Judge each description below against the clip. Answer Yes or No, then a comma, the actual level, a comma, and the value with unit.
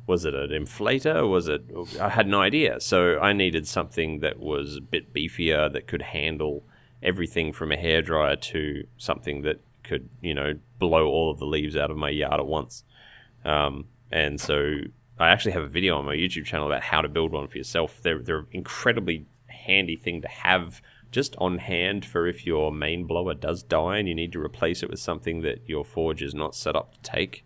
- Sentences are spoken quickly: Yes, fast, 210 wpm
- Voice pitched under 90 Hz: Yes, very low, 80 Hz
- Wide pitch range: No, average, 2.9 semitones